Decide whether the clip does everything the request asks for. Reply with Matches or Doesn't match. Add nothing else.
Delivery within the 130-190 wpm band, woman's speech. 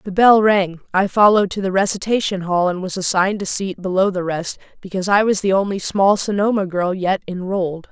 Doesn't match